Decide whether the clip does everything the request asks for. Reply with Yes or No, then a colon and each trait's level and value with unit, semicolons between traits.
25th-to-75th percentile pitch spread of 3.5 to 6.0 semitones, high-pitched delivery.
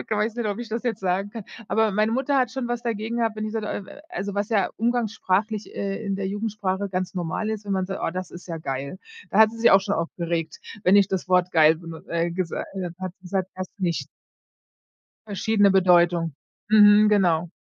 No: average, 3.1 semitones; high, 195 Hz